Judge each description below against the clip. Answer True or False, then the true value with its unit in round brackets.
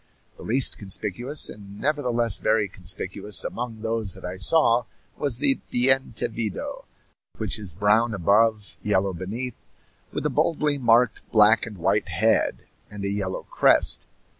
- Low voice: True (110 Hz)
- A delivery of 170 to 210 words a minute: False (140 wpm)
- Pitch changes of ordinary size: True (3.4 semitones)